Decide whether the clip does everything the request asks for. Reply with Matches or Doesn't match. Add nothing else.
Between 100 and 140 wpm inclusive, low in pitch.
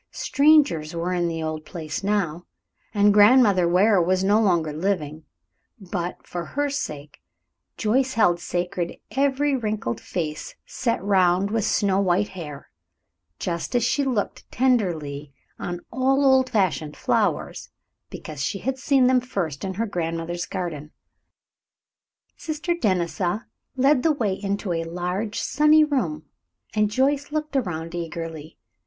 Doesn't match